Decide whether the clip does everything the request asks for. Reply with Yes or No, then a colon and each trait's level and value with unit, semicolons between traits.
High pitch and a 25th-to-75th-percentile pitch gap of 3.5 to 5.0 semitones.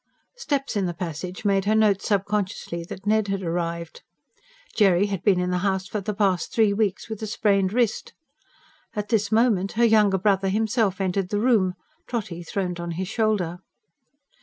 No: high, 200 Hz; average, 2.9 semitones